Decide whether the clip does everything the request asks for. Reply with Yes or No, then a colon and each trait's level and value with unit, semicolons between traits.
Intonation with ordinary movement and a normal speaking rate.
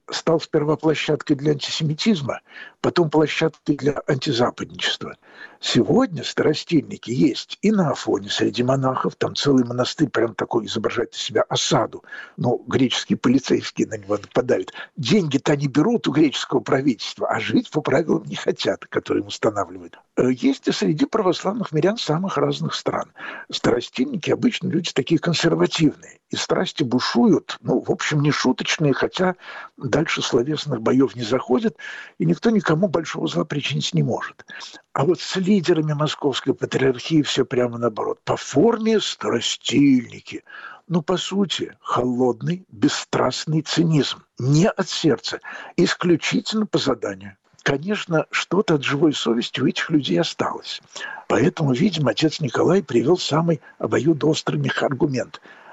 Yes: average, 4.6 semitones; average, 130 wpm